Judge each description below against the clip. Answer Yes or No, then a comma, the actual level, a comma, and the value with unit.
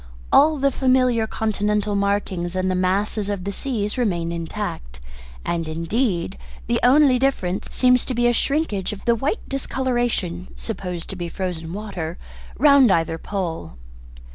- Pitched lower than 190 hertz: No, high, 205 Hz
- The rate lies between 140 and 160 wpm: Yes, average, 145 wpm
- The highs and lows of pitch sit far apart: Yes, wide, 6.1 semitones